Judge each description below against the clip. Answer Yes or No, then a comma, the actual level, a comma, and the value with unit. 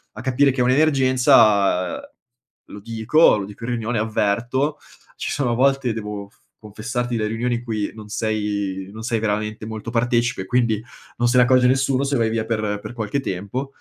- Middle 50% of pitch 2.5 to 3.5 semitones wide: Yes, average, 2.8 semitones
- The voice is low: Yes, low, 115 Hz